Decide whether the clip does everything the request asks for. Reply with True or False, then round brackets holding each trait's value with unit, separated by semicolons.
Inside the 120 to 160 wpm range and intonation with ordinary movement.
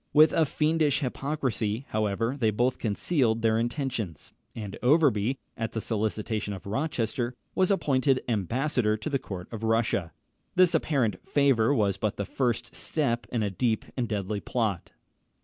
True (150 wpm; 4.3 semitones)